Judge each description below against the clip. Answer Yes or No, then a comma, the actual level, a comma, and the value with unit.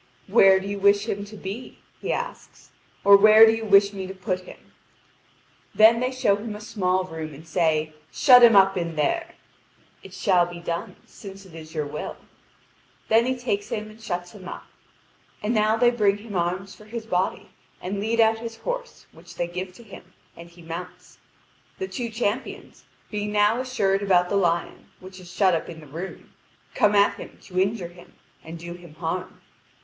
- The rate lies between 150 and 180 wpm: No, average, 195 wpm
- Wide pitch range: No, average, 3.8 semitones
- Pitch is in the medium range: No, high, 195 Hz